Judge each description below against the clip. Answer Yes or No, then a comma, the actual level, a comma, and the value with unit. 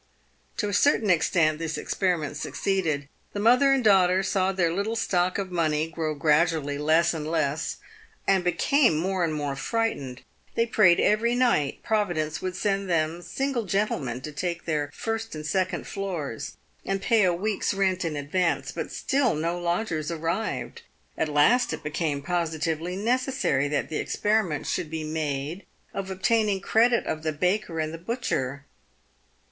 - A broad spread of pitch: No, average, 4.7 semitones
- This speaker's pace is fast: No, average, 165 wpm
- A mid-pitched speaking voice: Yes, medium, 175 Hz